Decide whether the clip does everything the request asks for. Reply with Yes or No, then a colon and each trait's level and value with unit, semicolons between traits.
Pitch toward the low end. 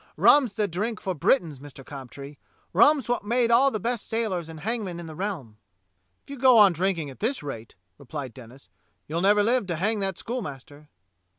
No: high, 190 Hz